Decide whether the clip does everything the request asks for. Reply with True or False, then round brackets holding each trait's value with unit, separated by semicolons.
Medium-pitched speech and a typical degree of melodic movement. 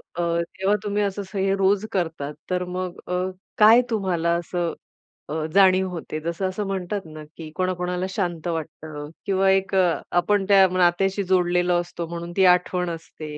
False (180 Hz; 2.2 semitones)